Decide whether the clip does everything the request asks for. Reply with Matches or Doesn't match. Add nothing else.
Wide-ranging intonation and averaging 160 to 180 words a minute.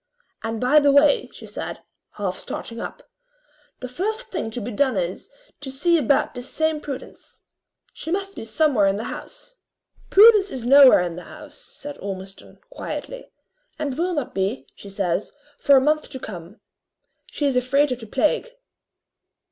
Matches